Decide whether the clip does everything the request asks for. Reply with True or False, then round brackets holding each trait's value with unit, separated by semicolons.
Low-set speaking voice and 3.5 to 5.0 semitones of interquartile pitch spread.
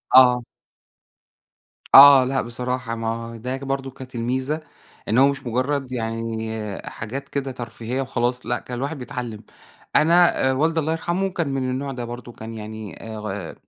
False (125 Hz; 3.0 semitones)